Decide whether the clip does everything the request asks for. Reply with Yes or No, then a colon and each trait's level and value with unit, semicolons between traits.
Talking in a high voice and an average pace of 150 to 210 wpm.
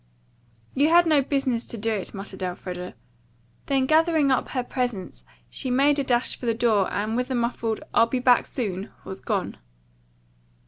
Yes: high, 245 Hz; average, 175 wpm